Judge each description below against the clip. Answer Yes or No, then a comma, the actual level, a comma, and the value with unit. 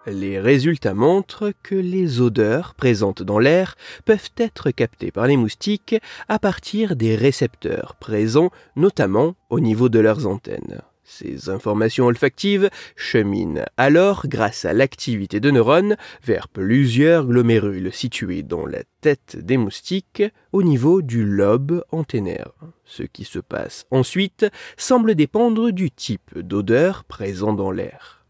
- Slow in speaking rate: Yes, slow, 135 wpm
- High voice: No, medium, 140 Hz